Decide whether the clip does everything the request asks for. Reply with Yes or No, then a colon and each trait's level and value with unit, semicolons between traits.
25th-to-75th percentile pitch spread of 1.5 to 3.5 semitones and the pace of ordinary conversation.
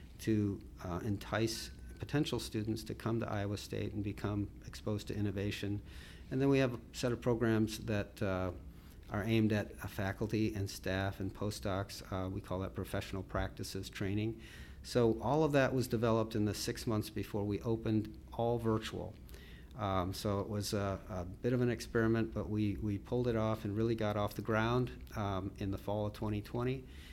Yes: narrow, 2.4 semitones; average, 185 wpm